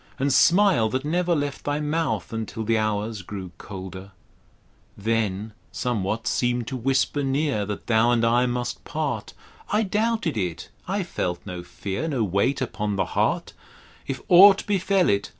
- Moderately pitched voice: No, low, 120 Hz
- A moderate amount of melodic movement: No, wide, 6.6 semitones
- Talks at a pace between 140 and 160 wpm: Yes, average, 155 wpm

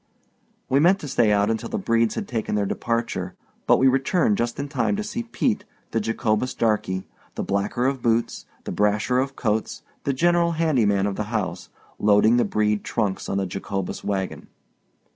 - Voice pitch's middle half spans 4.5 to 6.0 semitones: Yes, average, 4.8 semitones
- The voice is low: Yes, low, 115 Hz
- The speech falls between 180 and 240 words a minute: Yes, average, 185 wpm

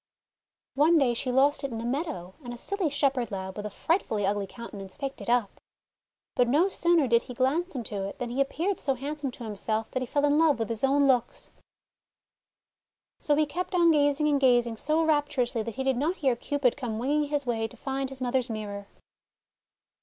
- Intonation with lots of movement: No, average, 3.9 semitones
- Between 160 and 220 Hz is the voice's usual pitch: No, very high, 265 Hz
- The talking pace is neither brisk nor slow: No, fast, 215 wpm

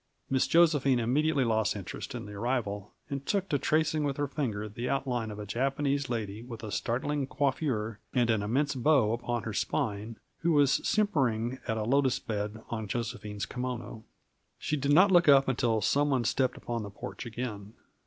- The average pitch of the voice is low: Yes, low, 125 Hz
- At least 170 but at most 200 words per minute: Yes, average, 185 wpm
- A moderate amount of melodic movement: Yes, average, 4.3 semitones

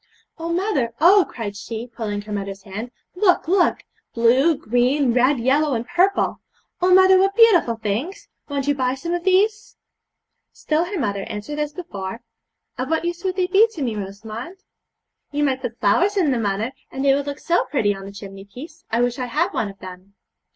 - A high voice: Yes, very high, 265 Hz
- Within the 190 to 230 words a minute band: Yes, average, 195 wpm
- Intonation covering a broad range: Yes, wide, 7.9 semitones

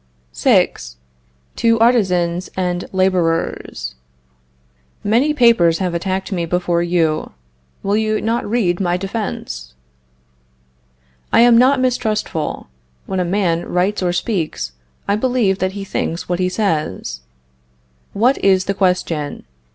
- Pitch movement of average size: Yes, average, 3.9 semitones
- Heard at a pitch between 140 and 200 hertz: Yes, medium, 185 Hz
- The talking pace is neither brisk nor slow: No, slow, 120 wpm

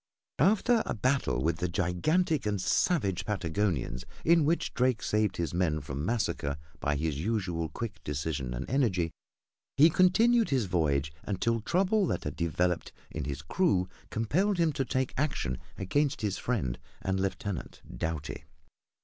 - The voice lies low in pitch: Yes, low, 100 Hz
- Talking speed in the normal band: Yes, average, 150 wpm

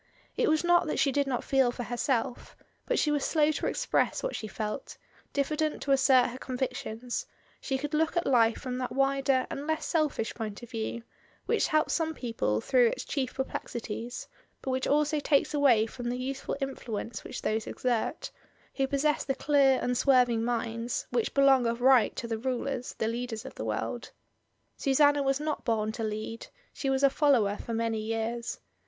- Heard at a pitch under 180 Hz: No, very high, 255 Hz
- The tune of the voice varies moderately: Yes, average, 3.3 semitones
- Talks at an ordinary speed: Yes, average, 185 wpm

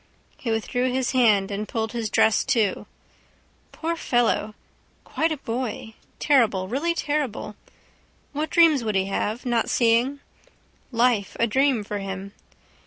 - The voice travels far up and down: No, average, 4.1 semitones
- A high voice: Yes, high, 235 Hz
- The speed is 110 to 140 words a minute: Yes, slow, 135 wpm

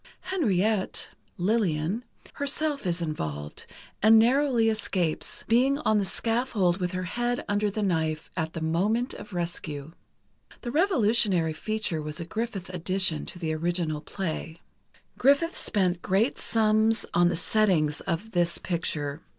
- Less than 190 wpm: Yes, slow, 135 wpm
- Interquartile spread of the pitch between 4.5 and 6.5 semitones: Yes, average, 5.2 semitones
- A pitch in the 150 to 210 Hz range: Yes, high, 190 Hz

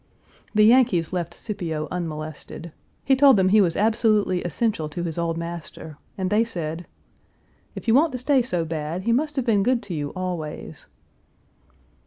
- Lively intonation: Yes, wide, 5.7 semitones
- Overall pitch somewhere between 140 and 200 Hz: Yes, medium, 185 Hz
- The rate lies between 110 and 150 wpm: No, average, 170 wpm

